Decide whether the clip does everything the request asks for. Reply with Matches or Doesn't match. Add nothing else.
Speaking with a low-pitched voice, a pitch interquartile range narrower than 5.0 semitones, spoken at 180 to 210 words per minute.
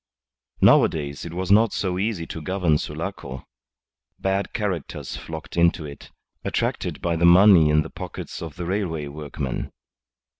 Doesn't match